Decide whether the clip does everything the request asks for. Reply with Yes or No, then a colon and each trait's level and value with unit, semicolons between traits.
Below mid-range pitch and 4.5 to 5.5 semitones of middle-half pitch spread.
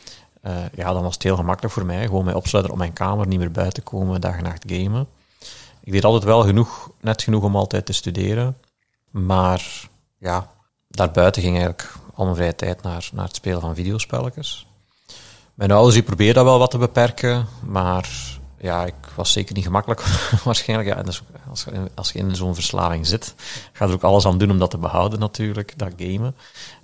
No: very low, 95 Hz; average, 3.5 semitones